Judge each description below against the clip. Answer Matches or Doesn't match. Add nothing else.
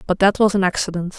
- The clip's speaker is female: Matches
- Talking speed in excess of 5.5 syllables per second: Matches